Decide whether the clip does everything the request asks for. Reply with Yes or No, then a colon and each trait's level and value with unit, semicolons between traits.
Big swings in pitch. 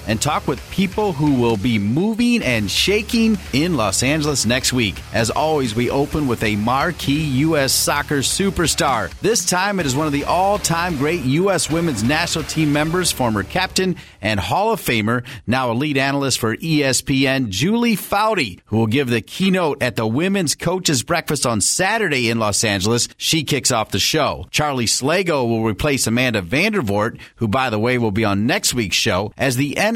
Yes: wide, 6.4 semitones